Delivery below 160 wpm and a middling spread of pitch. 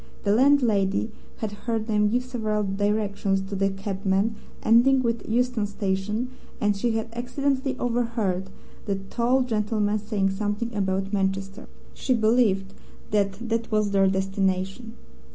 Yes: slow, 135 wpm; average, 3.1 semitones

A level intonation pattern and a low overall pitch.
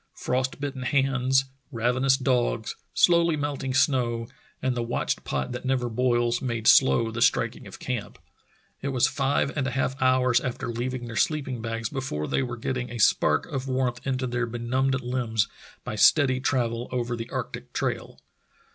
Yes: narrow, 2.0 semitones; low, 125 Hz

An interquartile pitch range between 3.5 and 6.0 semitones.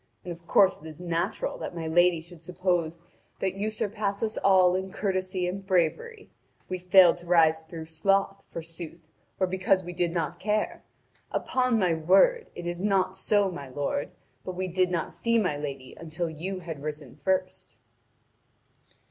No: average, 2.7 semitones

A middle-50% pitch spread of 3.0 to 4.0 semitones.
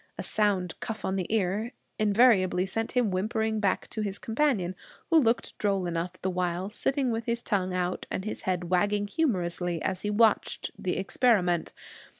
Yes: average, 3.4 semitones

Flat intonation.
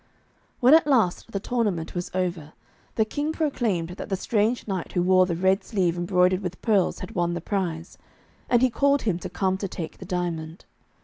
No: average, 3.8 semitones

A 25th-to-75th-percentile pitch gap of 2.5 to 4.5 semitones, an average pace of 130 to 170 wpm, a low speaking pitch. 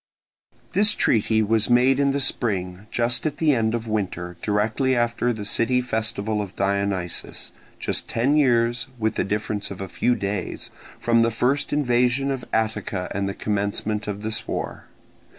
Yes: average, 3.1 semitones; average, 165 wpm; low, 110 Hz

